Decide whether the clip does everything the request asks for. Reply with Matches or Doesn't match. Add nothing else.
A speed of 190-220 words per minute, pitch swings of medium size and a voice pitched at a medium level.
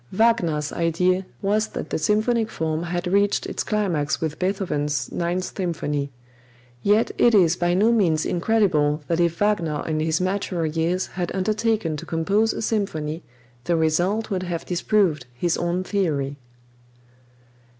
Doesn't match